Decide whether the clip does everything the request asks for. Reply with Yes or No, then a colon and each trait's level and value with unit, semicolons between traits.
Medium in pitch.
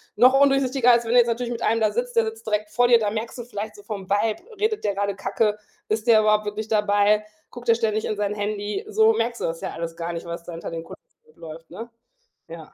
No: high, 215 Hz